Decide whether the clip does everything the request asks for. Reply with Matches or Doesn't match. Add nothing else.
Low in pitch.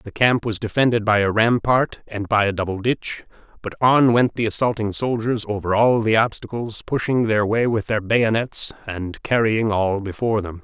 Matches